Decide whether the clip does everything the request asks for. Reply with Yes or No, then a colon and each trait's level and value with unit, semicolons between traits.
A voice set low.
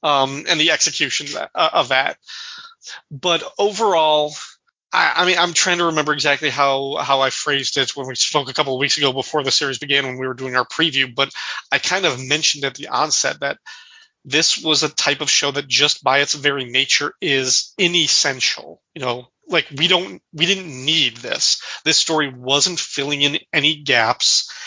No: medium, 145 Hz